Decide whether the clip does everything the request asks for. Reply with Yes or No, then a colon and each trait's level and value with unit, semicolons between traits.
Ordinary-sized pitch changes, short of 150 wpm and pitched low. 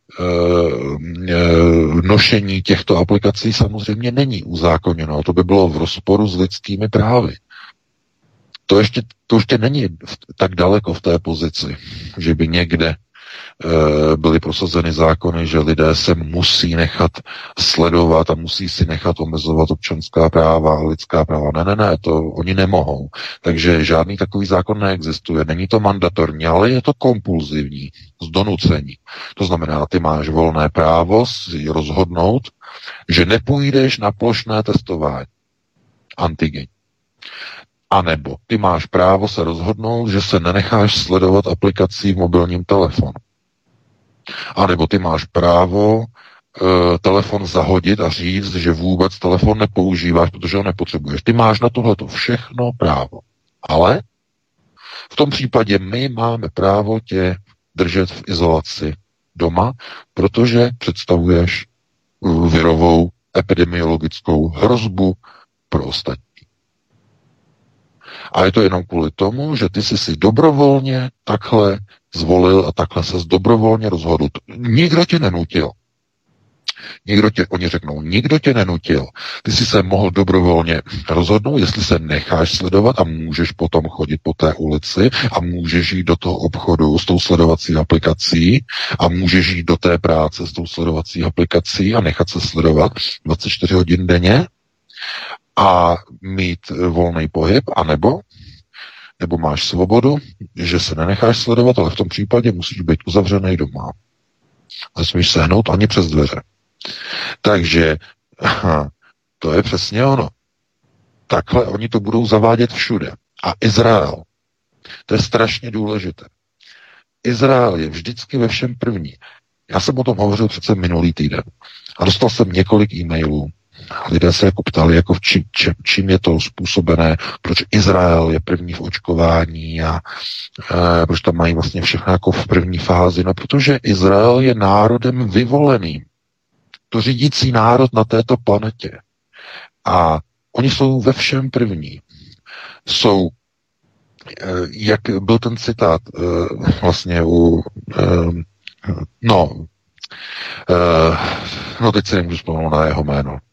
Yes: average, 4.4 semitones; average, 130 wpm; very low, 90 Hz